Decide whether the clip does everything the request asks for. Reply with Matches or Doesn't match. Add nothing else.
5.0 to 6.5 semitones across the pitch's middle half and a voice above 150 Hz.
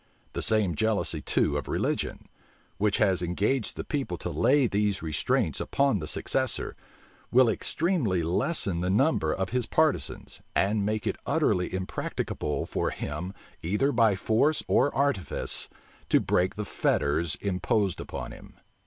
Doesn't match